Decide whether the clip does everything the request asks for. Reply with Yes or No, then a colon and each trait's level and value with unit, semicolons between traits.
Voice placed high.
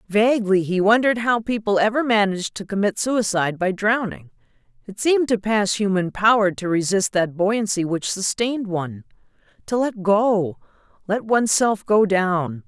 Yes: high, 205 Hz